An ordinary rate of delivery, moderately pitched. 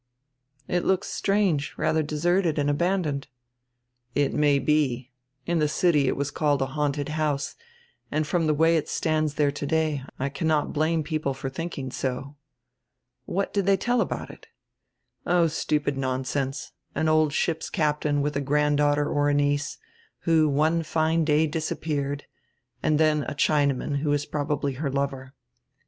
Yes: average, 155 wpm; medium, 150 Hz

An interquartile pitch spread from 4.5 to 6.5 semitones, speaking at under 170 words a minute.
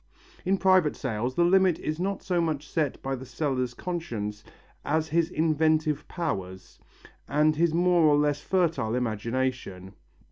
Yes: average, 5.0 semitones; average, 145 wpm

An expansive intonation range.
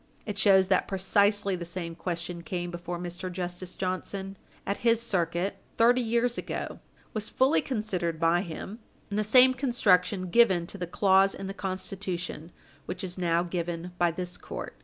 No: average, 2.7 semitones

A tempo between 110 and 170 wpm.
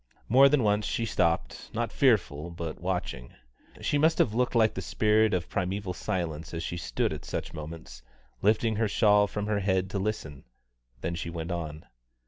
No: average, 180 wpm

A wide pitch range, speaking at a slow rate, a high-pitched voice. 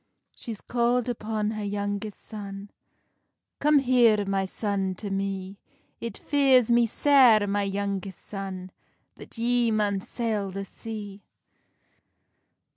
No: average, 3.0 semitones; slow, 120 wpm; high, 210 Hz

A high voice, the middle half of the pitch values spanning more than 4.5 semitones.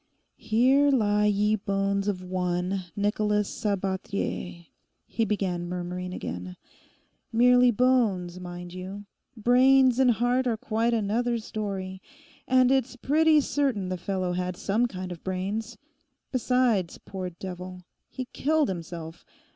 Yes: high, 205 Hz; average, 4.9 semitones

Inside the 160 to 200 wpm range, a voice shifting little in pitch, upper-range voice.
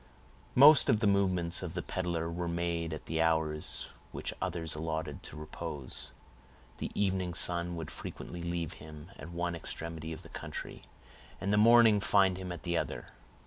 No: average, 170 wpm; narrow, 2.3 semitones; very low, 85 Hz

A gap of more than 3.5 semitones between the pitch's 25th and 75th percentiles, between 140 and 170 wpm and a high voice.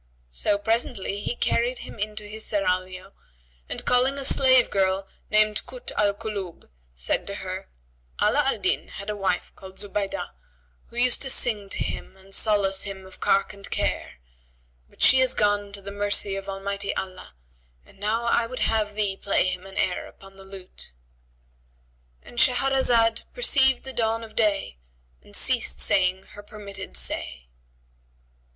No: average, 3.0 semitones; average, 160 wpm; high, 200 Hz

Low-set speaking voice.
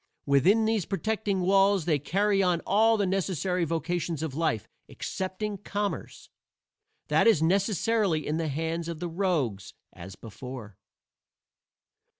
No: medium, 180 Hz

